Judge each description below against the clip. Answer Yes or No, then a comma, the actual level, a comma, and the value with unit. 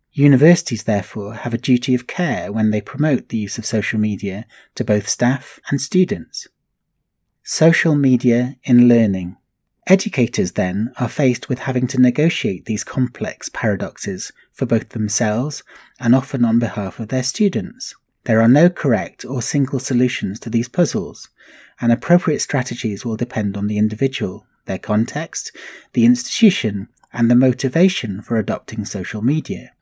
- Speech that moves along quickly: No, average, 150 wpm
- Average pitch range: Yes, average, 4.3 semitones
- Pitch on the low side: Yes, low, 125 Hz